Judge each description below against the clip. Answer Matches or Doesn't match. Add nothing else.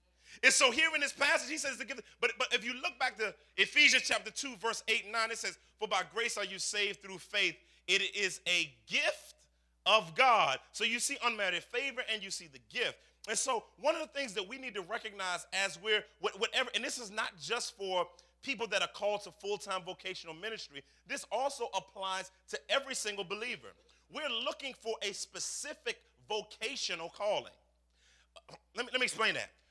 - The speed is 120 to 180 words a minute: Doesn't match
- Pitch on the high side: Matches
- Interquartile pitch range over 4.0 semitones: Matches